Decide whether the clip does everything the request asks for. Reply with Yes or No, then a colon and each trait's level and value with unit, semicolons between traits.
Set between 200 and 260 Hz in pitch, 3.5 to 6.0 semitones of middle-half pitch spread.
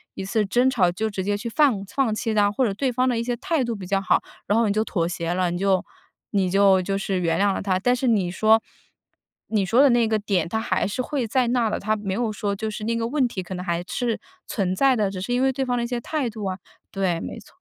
Yes: high, 215 Hz; average, 3.8 semitones